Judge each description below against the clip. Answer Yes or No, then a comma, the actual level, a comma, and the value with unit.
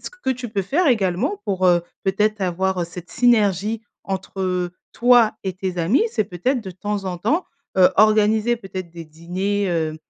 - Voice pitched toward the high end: Yes, high, 195 Hz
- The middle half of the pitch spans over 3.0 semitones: Yes, average, 3.4 semitones